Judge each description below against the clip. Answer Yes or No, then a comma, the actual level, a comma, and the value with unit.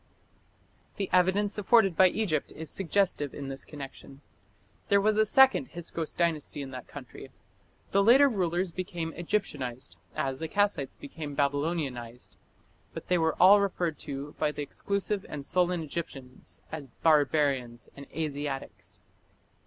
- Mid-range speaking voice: Yes, medium, 160 Hz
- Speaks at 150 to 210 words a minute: No, slow, 135 wpm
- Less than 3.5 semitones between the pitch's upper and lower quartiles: No, wide, 5.4 semitones